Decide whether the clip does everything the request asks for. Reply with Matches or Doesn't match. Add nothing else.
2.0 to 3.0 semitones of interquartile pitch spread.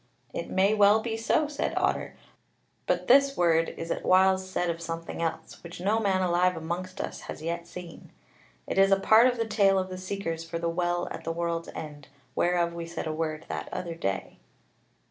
Matches